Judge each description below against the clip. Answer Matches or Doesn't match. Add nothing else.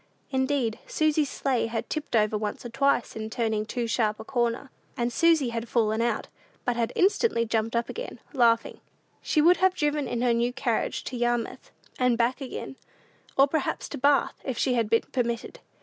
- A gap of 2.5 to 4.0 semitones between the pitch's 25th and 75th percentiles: Matches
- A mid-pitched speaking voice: Doesn't match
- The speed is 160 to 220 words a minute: Matches